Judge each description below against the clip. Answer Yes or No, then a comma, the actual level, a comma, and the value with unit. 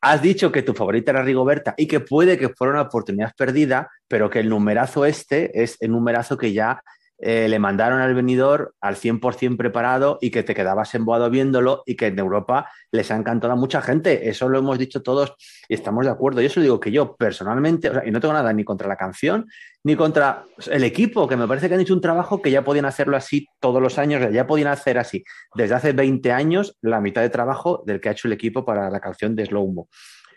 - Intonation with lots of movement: No, average, 4.0 semitones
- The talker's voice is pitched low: Yes, low, 130 Hz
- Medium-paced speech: No, fast, 235 wpm